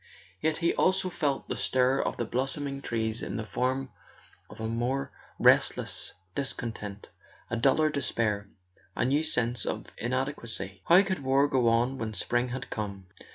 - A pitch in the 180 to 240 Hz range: No, low, 125 Hz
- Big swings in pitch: No, average, 3.4 semitones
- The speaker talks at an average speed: Yes, average, 160 wpm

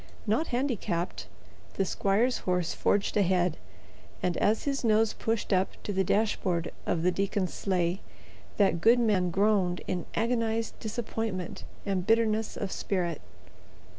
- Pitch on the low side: No, high, 200 Hz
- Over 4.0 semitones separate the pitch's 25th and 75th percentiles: No, average, 3.6 semitones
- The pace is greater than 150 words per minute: No, slow, 135 wpm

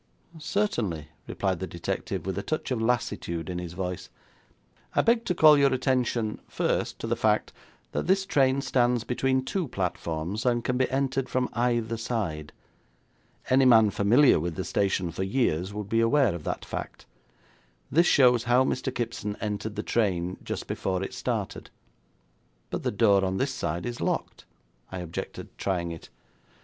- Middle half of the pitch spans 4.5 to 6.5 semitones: Yes, wide, 5.6 semitones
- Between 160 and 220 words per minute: Yes, average, 165 wpm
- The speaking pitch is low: Yes, low, 115 Hz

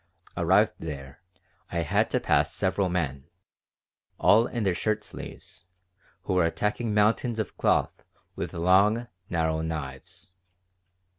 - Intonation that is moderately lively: Yes, average, 4.5 semitones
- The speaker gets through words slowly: Yes, slow, 125 wpm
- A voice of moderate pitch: No, very low, 90 Hz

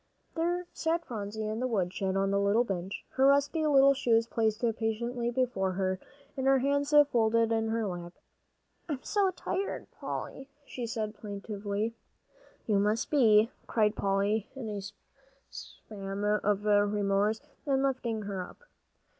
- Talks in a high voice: Yes, high, 220 Hz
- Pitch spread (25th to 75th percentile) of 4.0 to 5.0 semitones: Yes, average, 4.3 semitones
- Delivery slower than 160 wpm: Yes, average, 145 wpm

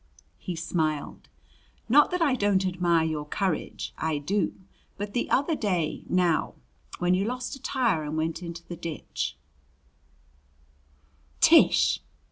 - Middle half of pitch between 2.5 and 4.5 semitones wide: No, average, 5.2 semitones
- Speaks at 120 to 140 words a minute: Yes, slow, 135 wpm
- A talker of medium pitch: Yes, medium, 170 Hz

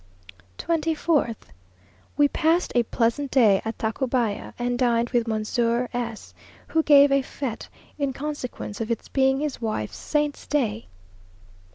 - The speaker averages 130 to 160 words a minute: Yes, slow, 135 wpm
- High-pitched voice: Yes, high, 245 Hz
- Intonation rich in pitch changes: No, average, 3.9 semitones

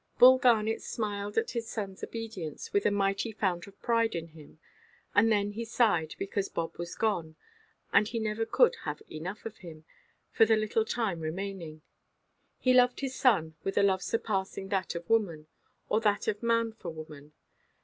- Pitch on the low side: No, high, 205 Hz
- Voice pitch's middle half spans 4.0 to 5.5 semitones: Yes, average, 4.7 semitones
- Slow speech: No, average, 175 wpm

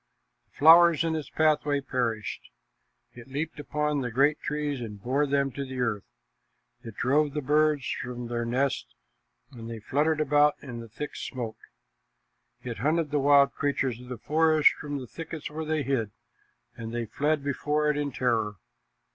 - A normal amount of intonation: Yes, average, 3.6 semitones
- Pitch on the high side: No, medium, 140 Hz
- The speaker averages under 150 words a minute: No, average, 165 wpm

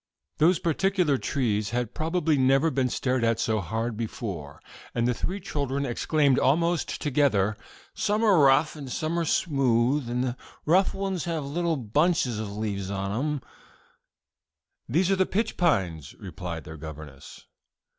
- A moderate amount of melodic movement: No, wide, 6.8 semitones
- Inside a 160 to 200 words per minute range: No, average, 150 wpm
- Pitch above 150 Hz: No, low, 135 Hz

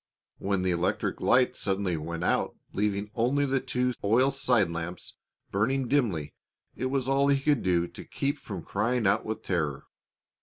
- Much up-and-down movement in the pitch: Yes, wide, 6.1 semitones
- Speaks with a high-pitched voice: No, low, 105 Hz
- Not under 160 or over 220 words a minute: Yes, average, 165 wpm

